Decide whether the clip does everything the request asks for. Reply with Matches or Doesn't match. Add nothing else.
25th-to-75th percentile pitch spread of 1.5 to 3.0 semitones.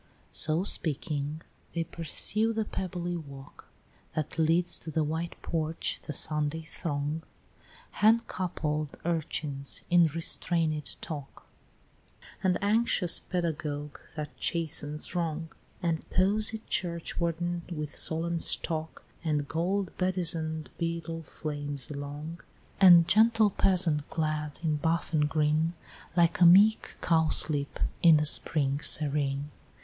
Matches